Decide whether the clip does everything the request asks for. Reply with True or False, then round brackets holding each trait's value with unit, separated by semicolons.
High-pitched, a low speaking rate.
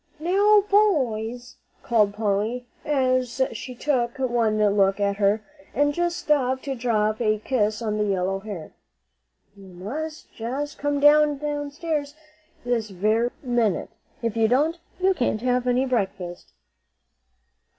True (245 Hz; 130 wpm)